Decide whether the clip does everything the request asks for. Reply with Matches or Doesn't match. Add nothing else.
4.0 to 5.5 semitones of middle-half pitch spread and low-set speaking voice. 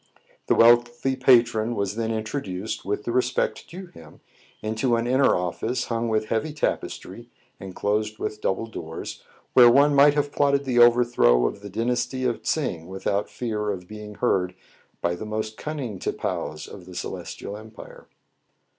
Doesn't match